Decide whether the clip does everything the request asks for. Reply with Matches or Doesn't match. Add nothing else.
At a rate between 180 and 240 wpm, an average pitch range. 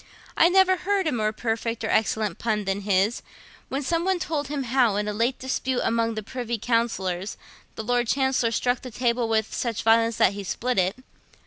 Matches